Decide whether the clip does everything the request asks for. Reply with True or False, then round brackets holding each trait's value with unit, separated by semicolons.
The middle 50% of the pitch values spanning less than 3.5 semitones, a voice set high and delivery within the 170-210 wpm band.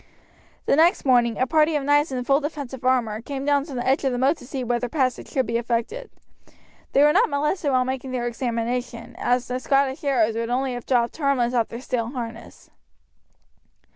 True (2.7 semitones; 255 Hz; 200 wpm)